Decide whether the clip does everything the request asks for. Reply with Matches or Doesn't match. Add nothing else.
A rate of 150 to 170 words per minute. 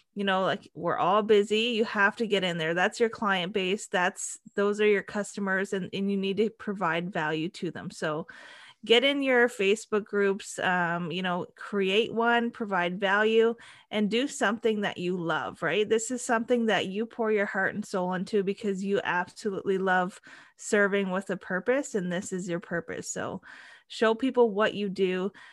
Doesn't match